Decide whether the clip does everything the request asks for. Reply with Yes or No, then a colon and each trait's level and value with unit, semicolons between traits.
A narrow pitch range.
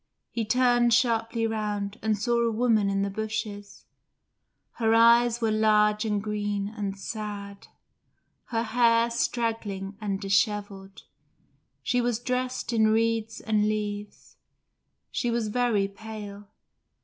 Yes: narrow, 2.1 semitones